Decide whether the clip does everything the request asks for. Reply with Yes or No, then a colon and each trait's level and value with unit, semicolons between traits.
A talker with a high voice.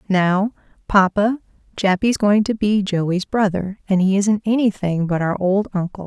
Yes: high, 195 Hz